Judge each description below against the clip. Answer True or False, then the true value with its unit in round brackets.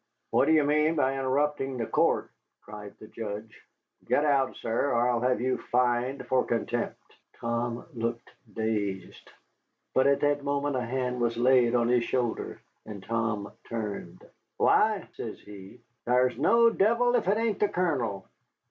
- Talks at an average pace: True (155 wpm)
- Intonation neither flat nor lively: True (3.6 semitones)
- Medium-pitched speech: False (125 Hz)